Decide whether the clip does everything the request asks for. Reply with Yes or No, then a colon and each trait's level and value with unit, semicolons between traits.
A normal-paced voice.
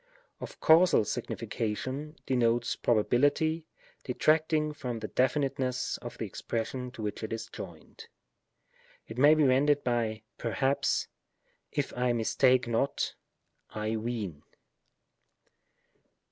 No: slow, 120 wpm